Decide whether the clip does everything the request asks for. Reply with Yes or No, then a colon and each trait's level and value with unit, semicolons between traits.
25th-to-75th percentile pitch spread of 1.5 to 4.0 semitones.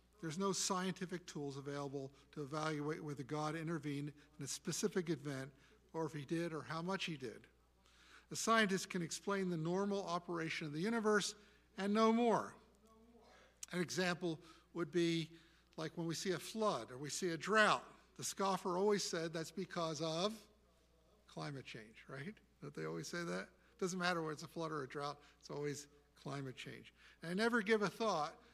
No: average, 4.6 semitones